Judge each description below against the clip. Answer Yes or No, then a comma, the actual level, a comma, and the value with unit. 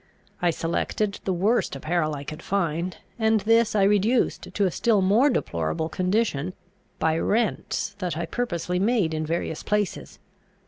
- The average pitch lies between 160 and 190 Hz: Yes, medium, 185 Hz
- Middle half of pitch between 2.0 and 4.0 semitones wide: No, average, 4.7 semitones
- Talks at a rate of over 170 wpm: No, average, 150 wpm